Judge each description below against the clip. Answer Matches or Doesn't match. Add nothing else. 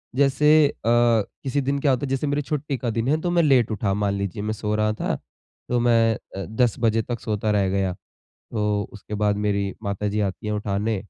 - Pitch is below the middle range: Matches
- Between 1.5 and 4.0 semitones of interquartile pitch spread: Doesn't match